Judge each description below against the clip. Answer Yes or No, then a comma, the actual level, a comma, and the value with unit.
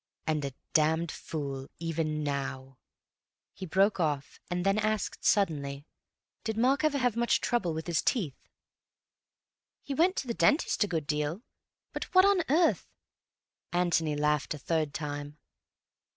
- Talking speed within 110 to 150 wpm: Yes, average, 145 wpm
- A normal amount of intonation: No, wide, 6.5 semitones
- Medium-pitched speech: Yes, medium, 165 Hz